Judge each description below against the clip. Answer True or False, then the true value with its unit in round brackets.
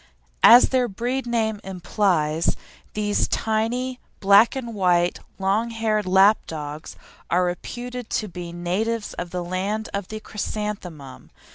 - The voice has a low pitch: False (205 Hz)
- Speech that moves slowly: True (130 wpm)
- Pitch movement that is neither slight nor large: True (4.1 semitones)